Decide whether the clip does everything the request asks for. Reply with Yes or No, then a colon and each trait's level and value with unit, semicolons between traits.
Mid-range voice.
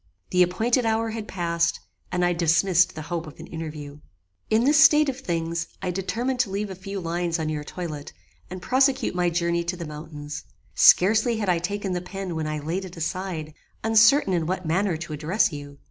Yes: medium, 180 Hz